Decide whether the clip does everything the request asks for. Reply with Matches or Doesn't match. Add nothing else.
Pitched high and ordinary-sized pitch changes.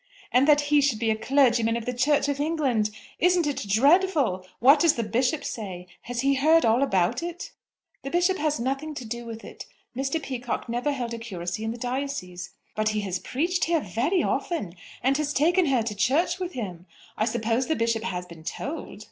Matches